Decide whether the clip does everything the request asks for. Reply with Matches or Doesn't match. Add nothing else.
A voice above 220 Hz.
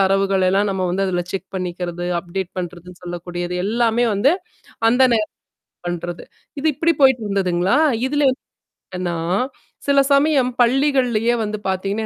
Doesn't match